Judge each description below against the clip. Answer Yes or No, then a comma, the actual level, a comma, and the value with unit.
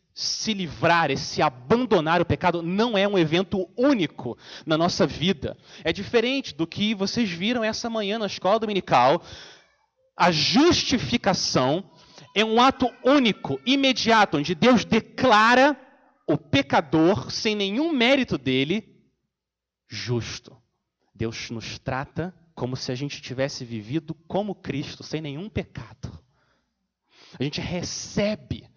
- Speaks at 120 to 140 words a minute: Yes, average, 125 wpm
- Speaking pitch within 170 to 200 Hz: Yes, high, 190 Hz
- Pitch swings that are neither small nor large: No, wide, 6.6 semitones